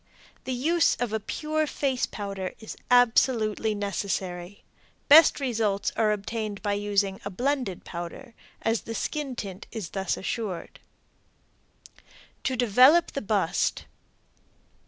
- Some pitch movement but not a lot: Yes, average, 4.2 semitones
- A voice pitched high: Yes, high, 220 Hz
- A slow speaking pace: Yes, slow, 120 wpm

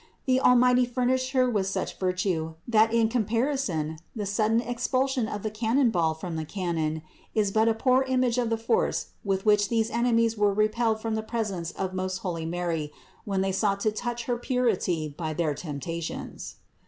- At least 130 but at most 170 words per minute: No, average, 180 wpm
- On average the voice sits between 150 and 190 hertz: No, high, 215 Hz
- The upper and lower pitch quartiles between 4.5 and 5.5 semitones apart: Yes, average, 4.8 semitones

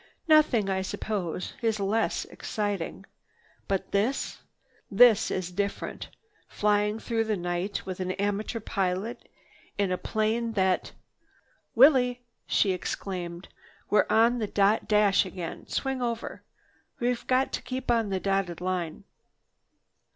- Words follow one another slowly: Yes, slow, 120 wpm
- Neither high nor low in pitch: No, high, 205 Hz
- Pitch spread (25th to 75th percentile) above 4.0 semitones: No, average, 3.4 semitones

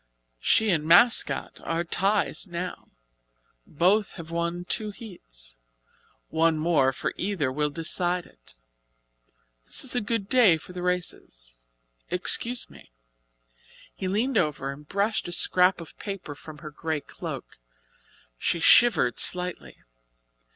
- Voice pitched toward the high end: No, medium, 175 Hz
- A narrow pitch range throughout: No, average, 4.6 semitones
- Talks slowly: Yes, slow, 130 wpm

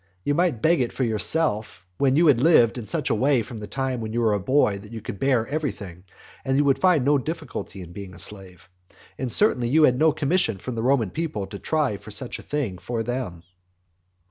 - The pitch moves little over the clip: No, wide, 5.5 semitones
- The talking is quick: Yes, fast, 225 wpm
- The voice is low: Yes, low, 125 Hz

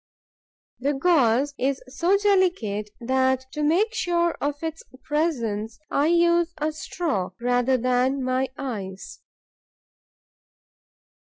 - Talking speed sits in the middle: No, slow, 105 wpm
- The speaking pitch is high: Yes, very high, 275 Hz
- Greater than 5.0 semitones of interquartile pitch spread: Yes, wide, 5.4 semitones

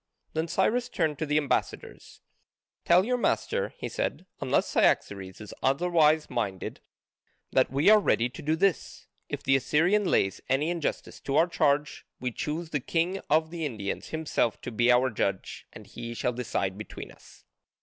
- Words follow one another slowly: No, average, 170 wpm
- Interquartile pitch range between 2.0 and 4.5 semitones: No, wide, 5.6 semitones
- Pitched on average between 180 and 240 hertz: No, medium, 150 Hz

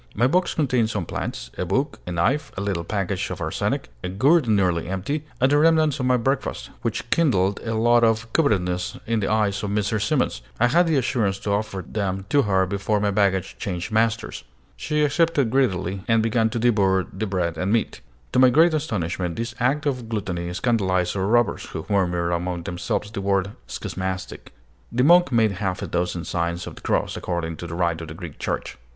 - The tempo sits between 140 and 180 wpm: No, average, 200 wpm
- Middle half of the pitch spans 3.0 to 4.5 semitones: No, average, 5.0 semitones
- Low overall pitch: Yes, low, 105 Hz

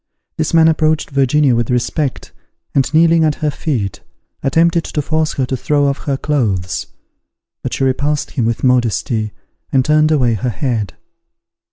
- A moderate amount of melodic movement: Yes, average, 4.0 semitones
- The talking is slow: No, average, 160 wpm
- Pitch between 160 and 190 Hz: No, medium, 140 Hz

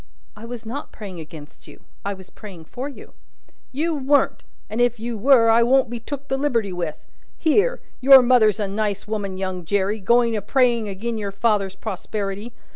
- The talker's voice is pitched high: Yes, high, 220 Hz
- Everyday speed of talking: Yes, average, 185 wpm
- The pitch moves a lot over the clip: No, average, 3.9 semitones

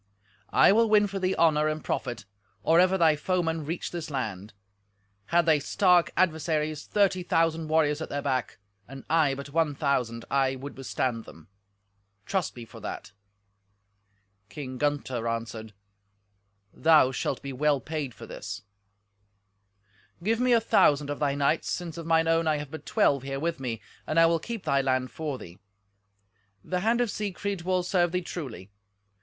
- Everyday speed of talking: Yes, average, 165 wpm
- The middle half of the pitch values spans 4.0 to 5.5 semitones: Yes, average, 4.7 semitones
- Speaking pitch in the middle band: Yes, medium, 150 Hz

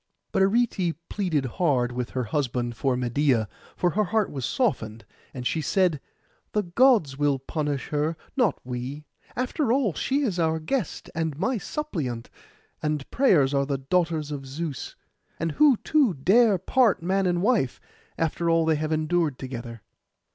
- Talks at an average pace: Yes, average, 160 wpm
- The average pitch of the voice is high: No, medium, 160 Hz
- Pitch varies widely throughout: Yes, wide, 6.3 semitones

